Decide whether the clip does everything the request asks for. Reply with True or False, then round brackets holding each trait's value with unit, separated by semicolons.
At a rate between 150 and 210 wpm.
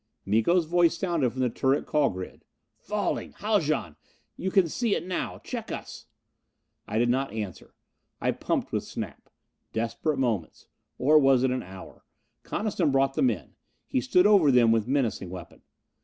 True (165 wpm)